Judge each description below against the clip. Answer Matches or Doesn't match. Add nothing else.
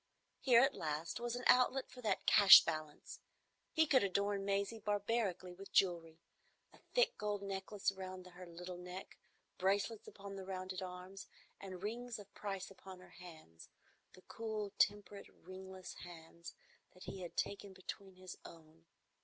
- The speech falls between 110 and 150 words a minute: Matches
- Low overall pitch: Doesn't match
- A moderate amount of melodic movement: Doesn't match